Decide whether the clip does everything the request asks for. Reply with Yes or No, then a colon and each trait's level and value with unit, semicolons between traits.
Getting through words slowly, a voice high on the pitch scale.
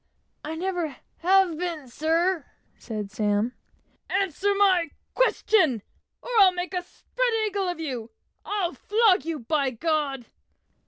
Yes: slow, 130 wpm; very high, 335 Hz